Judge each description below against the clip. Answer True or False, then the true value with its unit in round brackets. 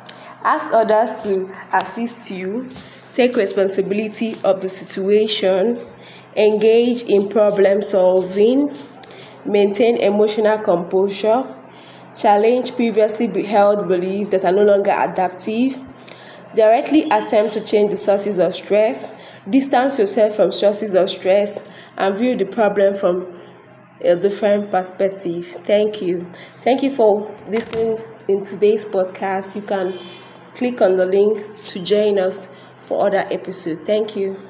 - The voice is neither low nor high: False (205 Hz)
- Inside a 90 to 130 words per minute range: True (125 wpm)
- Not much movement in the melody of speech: True (2.3 semitones)